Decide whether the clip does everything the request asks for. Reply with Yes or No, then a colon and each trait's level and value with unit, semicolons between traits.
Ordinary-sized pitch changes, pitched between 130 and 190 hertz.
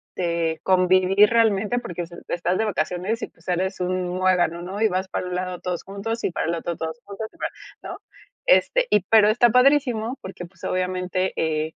Yes: average, 3.5 semitones; medium, 185 Hz